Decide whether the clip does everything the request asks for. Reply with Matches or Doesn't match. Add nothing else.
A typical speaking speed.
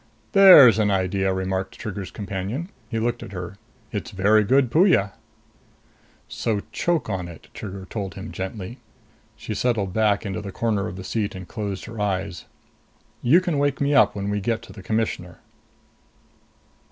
Matches